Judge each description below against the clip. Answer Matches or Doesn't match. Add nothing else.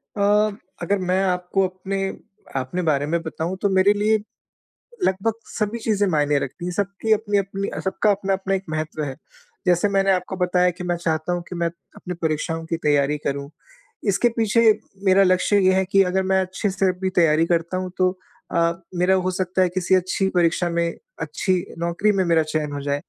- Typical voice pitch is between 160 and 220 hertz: Matches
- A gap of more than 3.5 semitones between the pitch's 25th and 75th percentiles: Doesn't match